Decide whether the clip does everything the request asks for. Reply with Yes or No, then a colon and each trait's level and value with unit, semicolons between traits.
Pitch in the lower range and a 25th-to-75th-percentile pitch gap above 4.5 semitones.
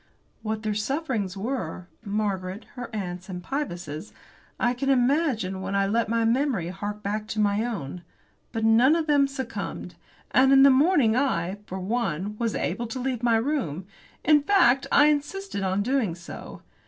No: high, 225 Hz; wide, 5.6 semitones